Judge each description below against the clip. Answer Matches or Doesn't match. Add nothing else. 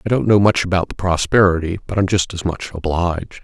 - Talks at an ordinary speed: Doesn't match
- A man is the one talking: Matches